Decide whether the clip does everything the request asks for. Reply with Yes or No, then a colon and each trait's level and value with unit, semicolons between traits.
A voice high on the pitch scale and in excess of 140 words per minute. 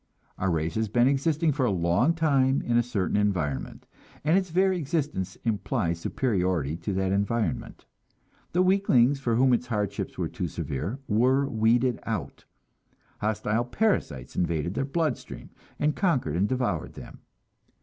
No: low, 120 Hz; average, 150 wpm